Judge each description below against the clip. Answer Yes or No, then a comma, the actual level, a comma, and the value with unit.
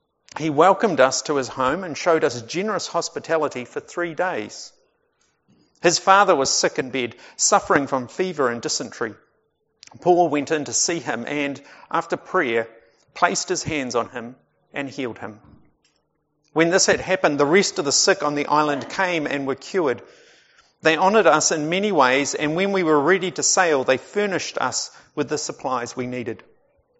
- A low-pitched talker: No, medium, 150 Hz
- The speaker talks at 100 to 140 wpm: No, average, 175 wpm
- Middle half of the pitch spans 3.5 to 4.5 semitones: No, wide, 5.4 semitones